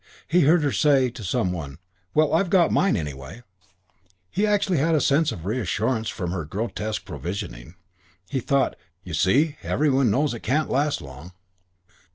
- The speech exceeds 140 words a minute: Yes, average, 170 wpm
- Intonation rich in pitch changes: Yes, wide, 8.8 semitones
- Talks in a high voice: No, low, 125 Hz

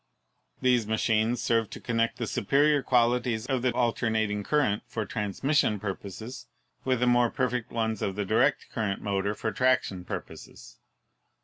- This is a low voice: Yes, low, 115 Hz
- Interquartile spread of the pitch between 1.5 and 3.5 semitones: Yes, average, 3.2 semitones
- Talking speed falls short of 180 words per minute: Yes, average, 150 wpm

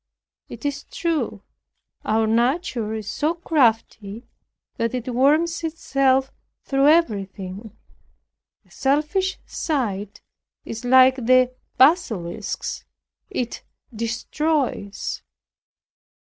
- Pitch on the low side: No, very high, 255 Hz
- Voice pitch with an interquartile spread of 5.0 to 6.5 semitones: Yes, wide, 5.4 semitones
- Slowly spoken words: Yes, slow, 85 wpm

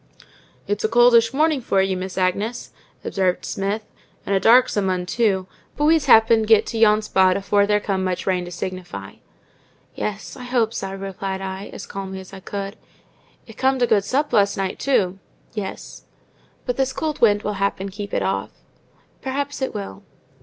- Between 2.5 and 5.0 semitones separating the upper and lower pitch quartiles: Yes, average, 3.5 semitones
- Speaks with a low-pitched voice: No, high, 205 Hz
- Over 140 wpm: Yes, average, 180 wpm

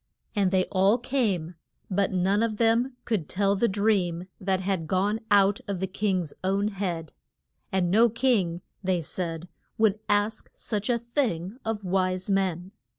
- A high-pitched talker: Yes, high, 195 Hz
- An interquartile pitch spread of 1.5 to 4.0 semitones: Yes, average, 2.7 semitones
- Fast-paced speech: No, average, 155 wpm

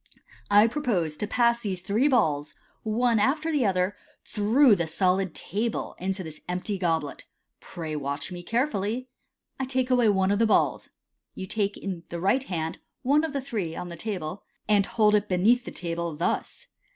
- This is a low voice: No, high, 205 Hz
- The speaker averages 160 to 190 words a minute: Yes, average, 180 wpm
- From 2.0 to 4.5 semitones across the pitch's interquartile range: No, average, 5.1 semitones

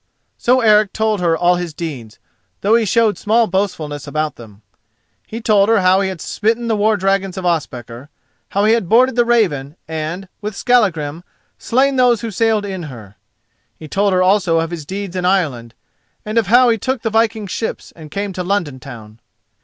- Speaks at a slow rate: No, average, 190 wpm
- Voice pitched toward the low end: No, high, 195 Hz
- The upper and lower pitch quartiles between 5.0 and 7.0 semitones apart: Yes, wide, 5.6 semitones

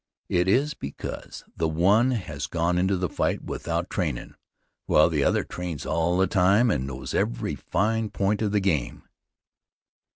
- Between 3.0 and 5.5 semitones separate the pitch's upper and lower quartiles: Yes, average, 4.0 semitones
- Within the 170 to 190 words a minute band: No, average, 160 wpm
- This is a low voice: Yes, very low, 90 Hz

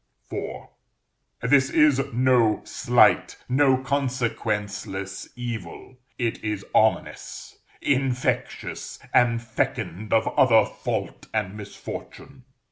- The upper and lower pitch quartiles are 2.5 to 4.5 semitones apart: Yes, average, 3.4 semitones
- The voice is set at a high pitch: No, low, 120 Hz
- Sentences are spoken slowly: Yes, slow, 90 wpm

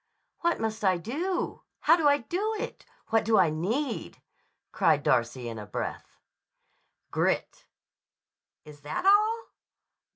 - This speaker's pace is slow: Yes, slow, 130 wpm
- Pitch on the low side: No, high, 225 Hz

